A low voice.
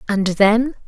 No: high, 220 Hz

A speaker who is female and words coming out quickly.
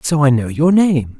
No: male; fast, 250 wpm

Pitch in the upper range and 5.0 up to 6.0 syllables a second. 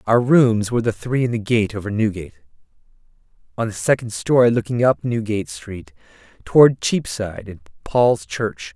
No: low, 110 Hz; 5.2 syllables/s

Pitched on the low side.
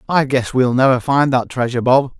Yes: low, 130 Hz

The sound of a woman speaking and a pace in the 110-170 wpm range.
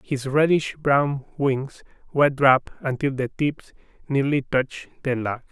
No: male; average, 140 wpm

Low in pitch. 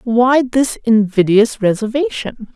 No: high, 230 Hz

